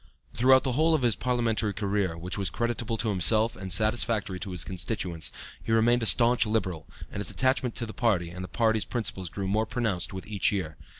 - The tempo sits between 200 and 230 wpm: Yes, fast, 205 wpm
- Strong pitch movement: No, average, 4.0 semitones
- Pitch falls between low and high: No, low, 110 Hz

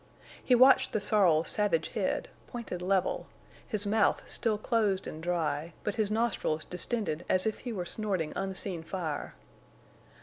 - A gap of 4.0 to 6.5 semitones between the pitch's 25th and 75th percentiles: Yes, average, 4.3 semitones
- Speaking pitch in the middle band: No, high, 195 Hz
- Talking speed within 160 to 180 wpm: No, average, 145 wpm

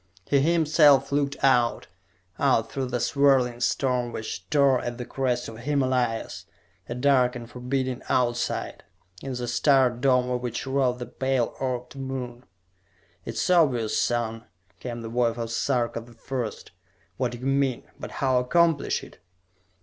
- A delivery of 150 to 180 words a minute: Yes, average, 155 wpm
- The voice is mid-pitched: No, low, 125 Hz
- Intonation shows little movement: Yes, narrow, 2.1 semitones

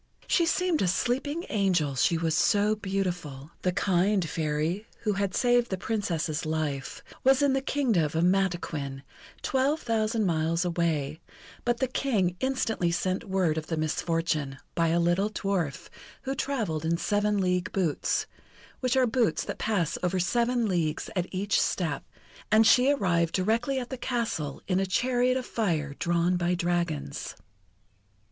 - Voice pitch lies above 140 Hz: Yes, medium, 185 Hz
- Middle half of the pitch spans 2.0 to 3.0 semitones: No, wide, 5.6 semitones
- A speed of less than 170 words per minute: Yes, average, 155 wpm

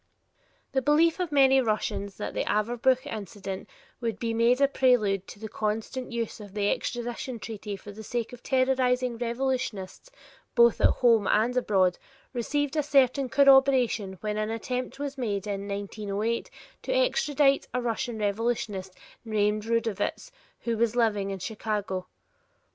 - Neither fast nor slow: Yes, average, 150 wpm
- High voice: Yes, high, 230 Hz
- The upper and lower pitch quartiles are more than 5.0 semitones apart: No, average, 3.7 semitones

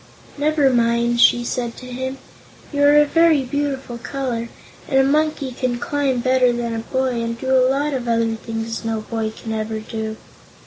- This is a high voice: Yes, very high, 250 Hz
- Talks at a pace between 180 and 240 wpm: Yes, average, 185 wpm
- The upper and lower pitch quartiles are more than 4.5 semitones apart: No, average, 2.8 semitones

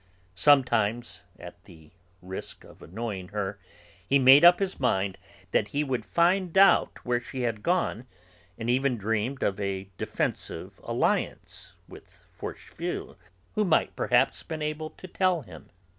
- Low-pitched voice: Yes, low, 125 Hz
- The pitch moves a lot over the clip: Yes, wide, 7.1 semitones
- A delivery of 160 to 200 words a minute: No, average, 145 wpm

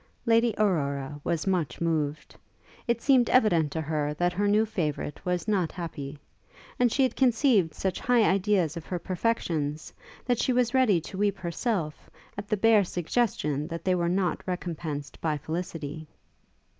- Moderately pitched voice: Yes, medium, 180 Hz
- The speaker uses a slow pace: No, average, 160 wpm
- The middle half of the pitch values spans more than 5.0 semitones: Yes, wide, 5.5 semitones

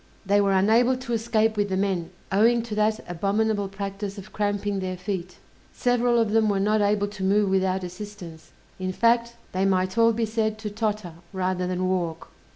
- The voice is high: Yes, high, 205 Hz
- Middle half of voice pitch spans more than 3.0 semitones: No, narrow, 2.6 semitones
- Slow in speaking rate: No, average, 185 wpm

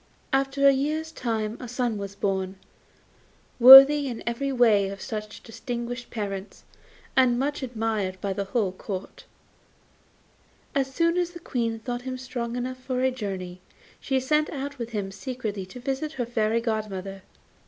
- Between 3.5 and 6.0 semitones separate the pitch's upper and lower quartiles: Yes, average, 4.2 semitones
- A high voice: Yes, high, 240 Hz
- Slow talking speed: No, average, 155 wpm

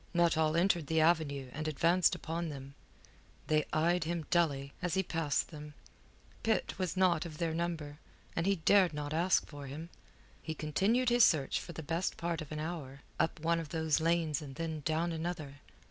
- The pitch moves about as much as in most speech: No, narrow, 2.2 semitones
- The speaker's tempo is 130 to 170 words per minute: No, average, 180 wpm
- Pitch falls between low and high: Yes, medium, 160 Hz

